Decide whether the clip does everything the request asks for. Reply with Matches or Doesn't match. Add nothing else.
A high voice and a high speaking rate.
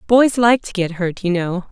Matches